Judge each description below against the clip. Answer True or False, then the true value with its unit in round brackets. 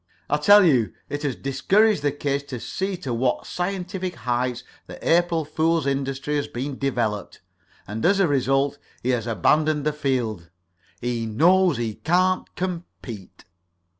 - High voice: False (140 Hz)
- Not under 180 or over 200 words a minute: False (150 wpm)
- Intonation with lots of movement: True (5.9 semitones)